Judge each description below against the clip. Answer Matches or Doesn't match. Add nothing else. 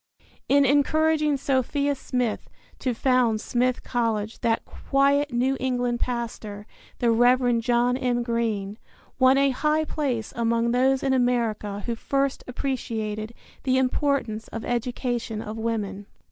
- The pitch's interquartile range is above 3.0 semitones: Doesn't match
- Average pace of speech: Doesn't match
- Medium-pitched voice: Doesn't match